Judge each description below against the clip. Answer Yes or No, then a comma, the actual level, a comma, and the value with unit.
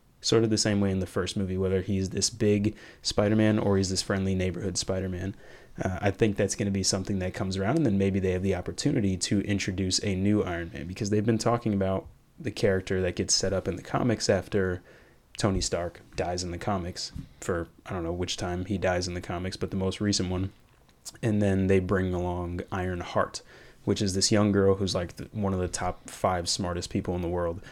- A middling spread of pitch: No, narrow, 2.0 semitones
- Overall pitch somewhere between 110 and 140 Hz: No, very low, 95 Hz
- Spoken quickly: Yes, fast, 235 wpm